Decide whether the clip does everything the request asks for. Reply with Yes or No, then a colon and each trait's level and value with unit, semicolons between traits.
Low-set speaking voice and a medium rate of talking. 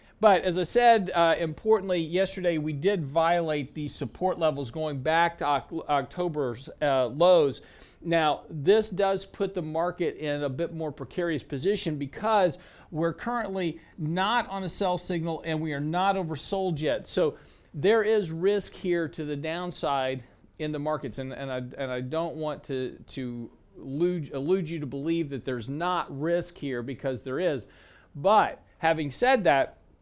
No: medium, 165 Hz; average, 160 wpm